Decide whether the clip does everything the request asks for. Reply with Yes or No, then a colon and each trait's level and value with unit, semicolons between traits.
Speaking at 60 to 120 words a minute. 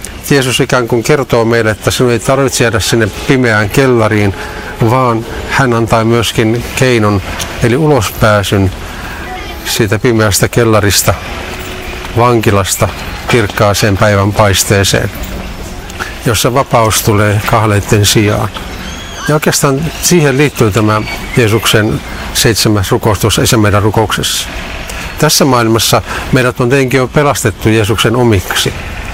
Yes: average, 105 wpm